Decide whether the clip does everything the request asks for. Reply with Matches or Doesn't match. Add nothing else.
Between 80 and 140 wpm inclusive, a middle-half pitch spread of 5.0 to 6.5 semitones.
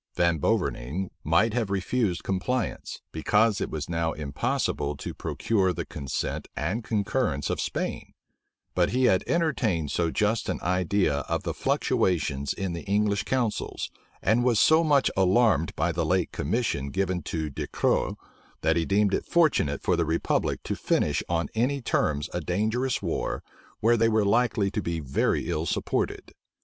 Doesn't match